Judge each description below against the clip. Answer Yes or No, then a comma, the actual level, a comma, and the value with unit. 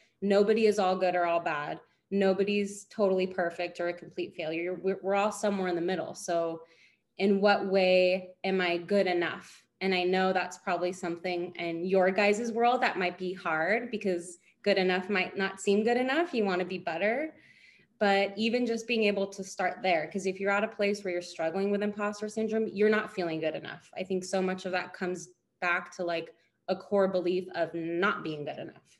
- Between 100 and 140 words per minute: No, fast, 205 wpm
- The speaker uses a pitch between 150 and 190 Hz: Yes, medium, 185 Hz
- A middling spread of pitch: No, narrow, 2.3 semitones